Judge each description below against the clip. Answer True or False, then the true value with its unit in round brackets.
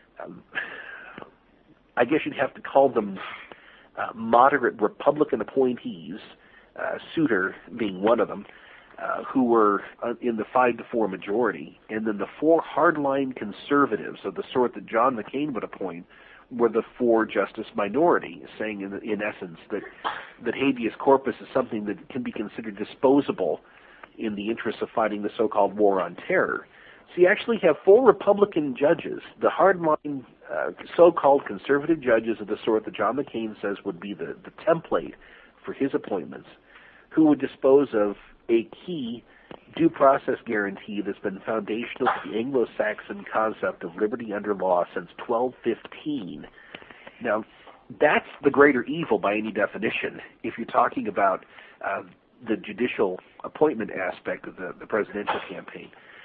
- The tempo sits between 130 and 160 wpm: True (155 wpm)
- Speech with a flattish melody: False (5.5 semitones)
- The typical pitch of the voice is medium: False (125 Hz)